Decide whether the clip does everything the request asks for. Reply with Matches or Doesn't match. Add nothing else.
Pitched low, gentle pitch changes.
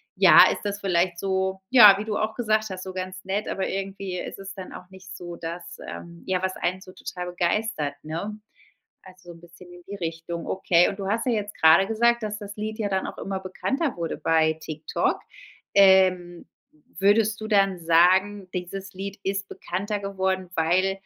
Doesn't match